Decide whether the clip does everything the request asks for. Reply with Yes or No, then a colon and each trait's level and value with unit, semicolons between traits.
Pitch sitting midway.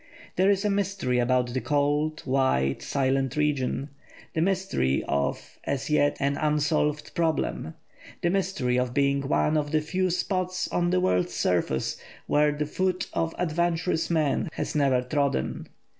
Yes: medium, 150 Hz